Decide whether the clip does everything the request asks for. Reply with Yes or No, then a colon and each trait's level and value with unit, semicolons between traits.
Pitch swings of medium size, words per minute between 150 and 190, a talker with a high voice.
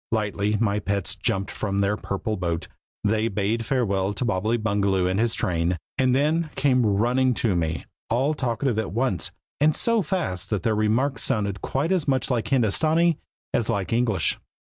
No: average, 4.6 semitones; average, 170 wpm; low, 110 Hz